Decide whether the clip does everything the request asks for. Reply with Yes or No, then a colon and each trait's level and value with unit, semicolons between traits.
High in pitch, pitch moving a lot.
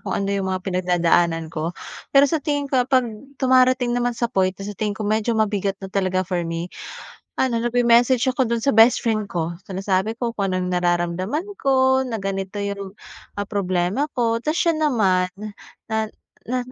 No: high, 205 Hz; average, 4.8 semitones